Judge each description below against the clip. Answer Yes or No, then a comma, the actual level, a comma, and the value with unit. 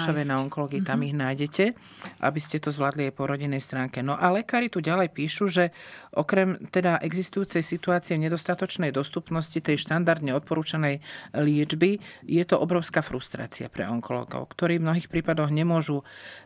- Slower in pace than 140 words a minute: No, average, 155 wpm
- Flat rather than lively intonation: No, average, 3.5 semitones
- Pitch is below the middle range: No, medium, 160 Hz